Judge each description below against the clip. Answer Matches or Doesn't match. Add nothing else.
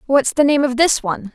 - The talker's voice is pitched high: Matches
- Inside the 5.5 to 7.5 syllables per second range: Matches